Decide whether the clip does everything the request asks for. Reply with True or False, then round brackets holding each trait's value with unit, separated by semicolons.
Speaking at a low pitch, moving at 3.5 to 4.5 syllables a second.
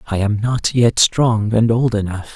True (110 Hz; 4.1 syllables/s)